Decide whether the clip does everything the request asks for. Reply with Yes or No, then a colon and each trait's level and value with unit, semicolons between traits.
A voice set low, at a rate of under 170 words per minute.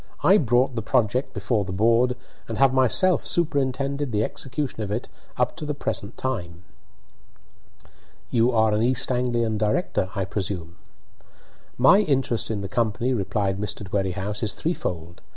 Yes: low, 115 Hz; average, 150 wpm